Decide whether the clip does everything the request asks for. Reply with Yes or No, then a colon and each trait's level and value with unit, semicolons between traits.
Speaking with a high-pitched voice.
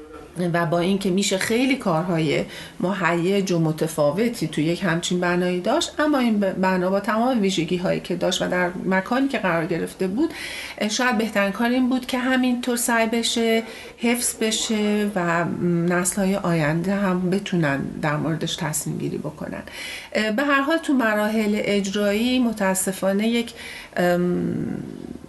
Yes: high, 195 Hz